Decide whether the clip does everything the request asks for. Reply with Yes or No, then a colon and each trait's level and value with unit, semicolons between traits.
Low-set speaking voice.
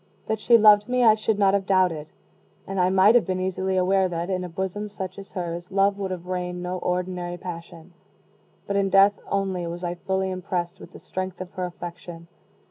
No: medium, 185 Hz